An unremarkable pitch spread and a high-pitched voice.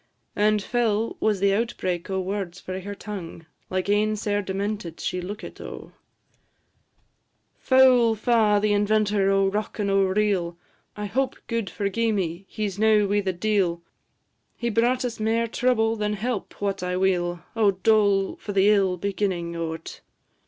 No: narrow, 2.3 semitones; high, 205 Hz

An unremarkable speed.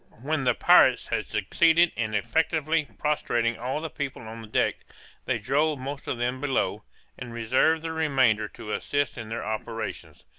Yes: average, 170 wpm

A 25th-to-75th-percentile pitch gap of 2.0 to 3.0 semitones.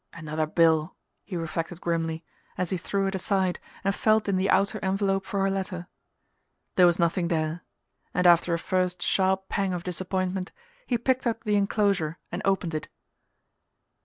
Yes: narrow, 2.5 semitones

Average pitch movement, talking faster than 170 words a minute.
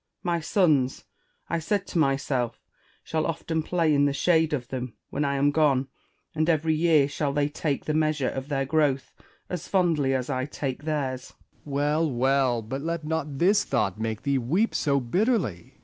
Yes: average, 3.2 semitones; average, 180 wpm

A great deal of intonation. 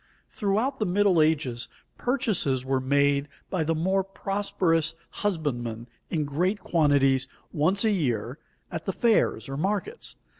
Yes: wide, 6.1 semitones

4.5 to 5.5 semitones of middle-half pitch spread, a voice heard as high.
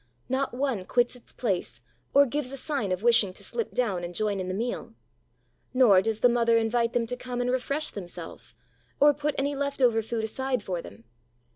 No: average, 4.1 semitones; high, 240 Hz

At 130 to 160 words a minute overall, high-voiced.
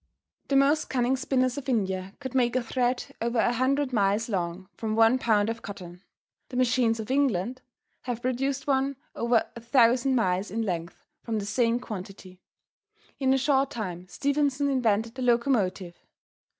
Yes: average, 155 wpm; high, 235 Hz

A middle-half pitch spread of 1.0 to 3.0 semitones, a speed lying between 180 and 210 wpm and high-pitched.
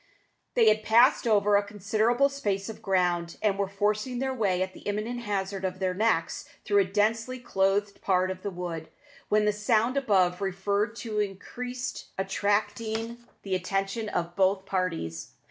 No: average, 2.7 semitones; average, 165 wpm; high, 205 Hz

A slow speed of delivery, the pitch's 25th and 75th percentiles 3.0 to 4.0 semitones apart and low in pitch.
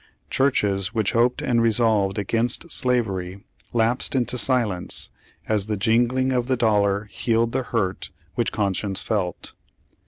Yes: slow, 130 wpm; average, 3.5 semitones; low, 115 Hz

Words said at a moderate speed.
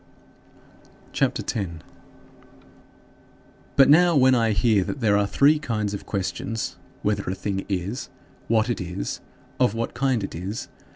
Yes: average, 150 wpm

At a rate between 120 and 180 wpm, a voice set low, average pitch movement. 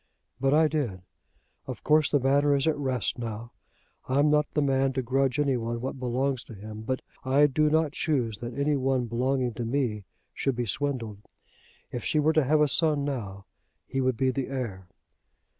No: average, 190 wpm; low, 130 Hz; average, 3.3 semitones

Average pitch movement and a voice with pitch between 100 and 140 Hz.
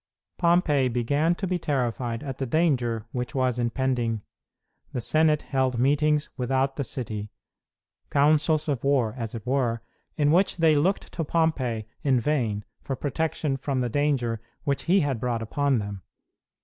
Yes: average, 4.0 semitones; low, 135 Hz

